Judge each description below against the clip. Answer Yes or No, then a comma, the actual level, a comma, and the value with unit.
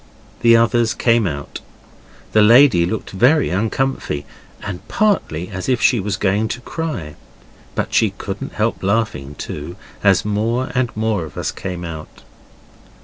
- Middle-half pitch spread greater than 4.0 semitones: Yes, average, 5.1 semitones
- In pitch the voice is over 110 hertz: No, low, 105 Hz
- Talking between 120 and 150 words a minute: Yes, average, 145 wpm